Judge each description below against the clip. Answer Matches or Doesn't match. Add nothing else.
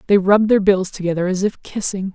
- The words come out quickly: Matches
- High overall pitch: Matches